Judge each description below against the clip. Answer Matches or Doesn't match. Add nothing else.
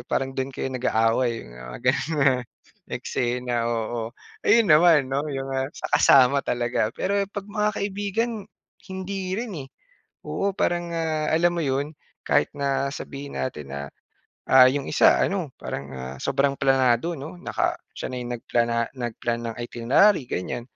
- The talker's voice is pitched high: Doesn't match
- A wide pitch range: Matches